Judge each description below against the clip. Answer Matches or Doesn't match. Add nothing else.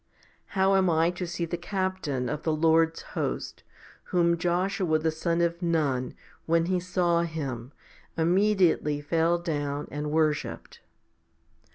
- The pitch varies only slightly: Matches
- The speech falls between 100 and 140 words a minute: Matches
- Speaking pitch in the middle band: Matches